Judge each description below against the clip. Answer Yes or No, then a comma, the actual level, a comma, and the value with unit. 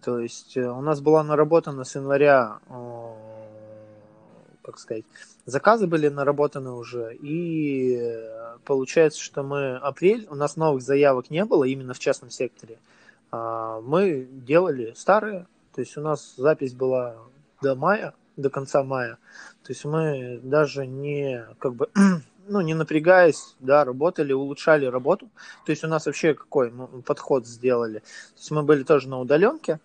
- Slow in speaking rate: No, average, 145 wpm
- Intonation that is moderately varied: Yes, average, 3.5 semitones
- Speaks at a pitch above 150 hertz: No, medium, 140 Hz